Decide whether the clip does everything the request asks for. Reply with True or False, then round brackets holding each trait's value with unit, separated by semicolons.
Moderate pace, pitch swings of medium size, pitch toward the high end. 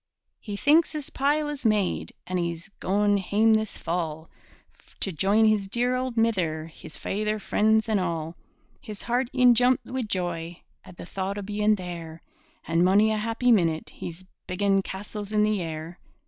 True (170 wpm; 4.0 semitones; 205 Hz)